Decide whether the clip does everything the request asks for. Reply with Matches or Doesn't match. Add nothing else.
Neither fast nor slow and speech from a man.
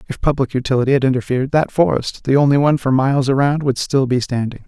Matches